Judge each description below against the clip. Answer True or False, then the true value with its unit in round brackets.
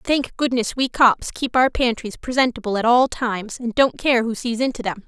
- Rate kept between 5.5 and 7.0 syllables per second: False (5.1 syllables/s)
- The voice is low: False (240 Hz)